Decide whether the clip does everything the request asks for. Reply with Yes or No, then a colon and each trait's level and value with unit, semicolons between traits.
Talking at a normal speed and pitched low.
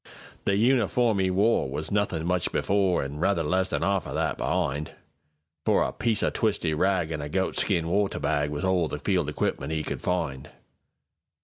Yes: average, 155 wpm; very low, 90 Hz